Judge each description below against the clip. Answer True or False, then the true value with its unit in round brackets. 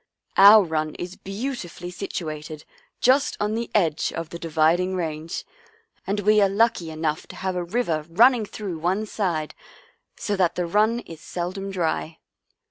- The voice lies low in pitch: False (180 Hz)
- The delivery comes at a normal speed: True (165 wpm)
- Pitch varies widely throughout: False (4.3 semitones)